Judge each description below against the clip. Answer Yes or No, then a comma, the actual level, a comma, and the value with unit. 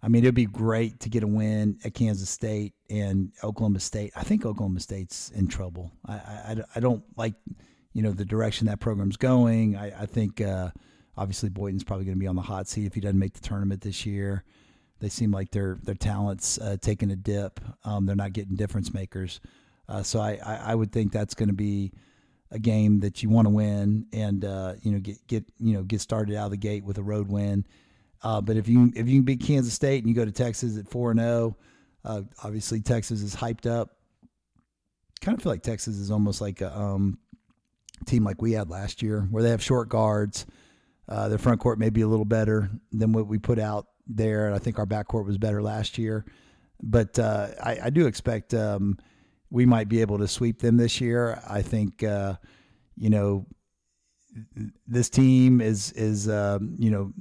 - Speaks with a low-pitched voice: Yes, low, 105 Hz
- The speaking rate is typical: No, fast, 215 wpm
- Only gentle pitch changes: Yes, narrow, 2.1 semitones